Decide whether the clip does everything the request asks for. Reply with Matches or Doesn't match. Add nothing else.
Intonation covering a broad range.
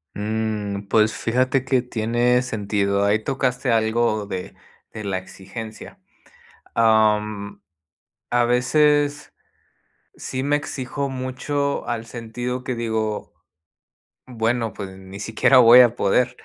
Doesn't match